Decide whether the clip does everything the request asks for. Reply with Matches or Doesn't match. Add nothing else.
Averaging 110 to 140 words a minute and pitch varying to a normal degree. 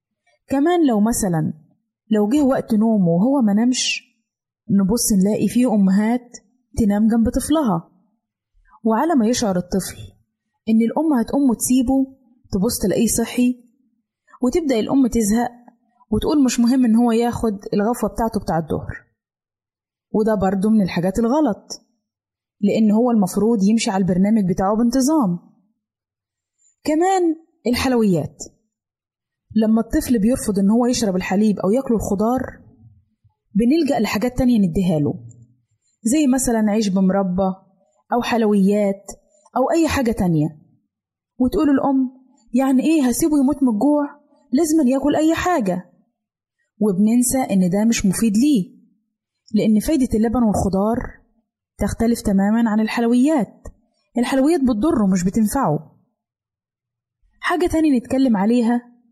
Matches